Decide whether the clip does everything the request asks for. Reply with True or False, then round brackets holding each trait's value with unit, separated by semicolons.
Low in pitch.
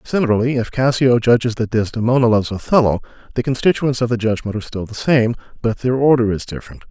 True (120 Hz)